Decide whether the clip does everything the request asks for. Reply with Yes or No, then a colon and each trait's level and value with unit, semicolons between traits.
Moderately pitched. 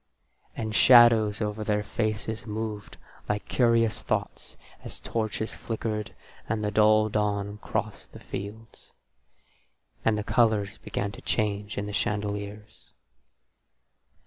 No: low, 105 Hz